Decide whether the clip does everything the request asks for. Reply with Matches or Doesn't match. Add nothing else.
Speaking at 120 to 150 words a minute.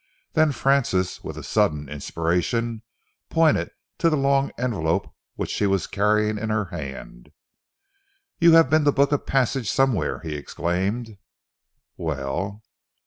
Matches